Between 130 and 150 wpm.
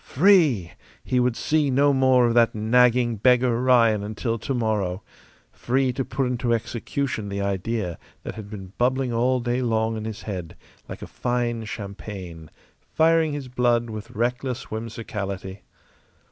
Yes: average, 145 wpm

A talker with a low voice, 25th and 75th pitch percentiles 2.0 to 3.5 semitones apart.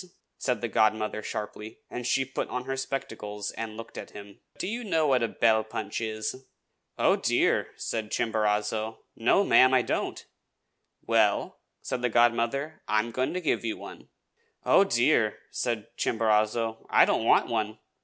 Yes: low, 115 Hz; average, 2.7 semitones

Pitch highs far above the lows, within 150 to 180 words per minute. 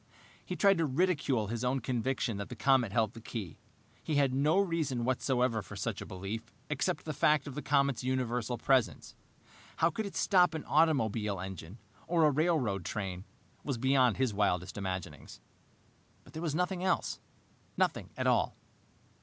Yes: wide, 5.8 semitones; average, 170 wpm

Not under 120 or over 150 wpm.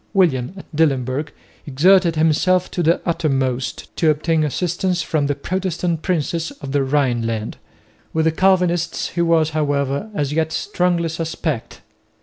Yes: slow, 135 wpm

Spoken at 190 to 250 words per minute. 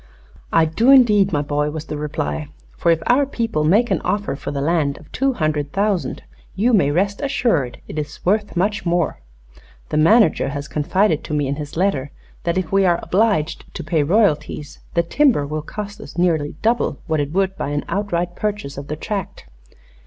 Yes: average, 195 wpm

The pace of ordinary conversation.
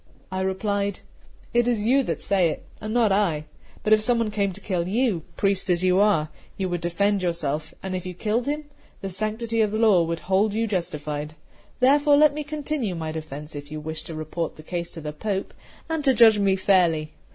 No: fast, 210 wpm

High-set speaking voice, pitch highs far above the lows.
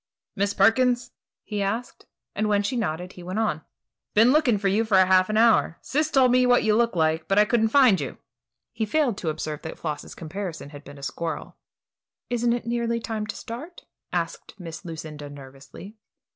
Yes: high, 210 Hz; wide, 6.2 semitones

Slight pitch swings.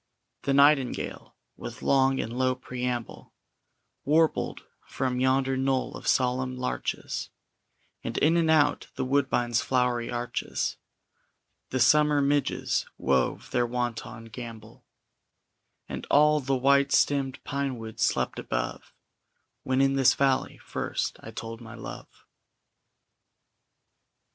Yes: narrow, 2.3 semitones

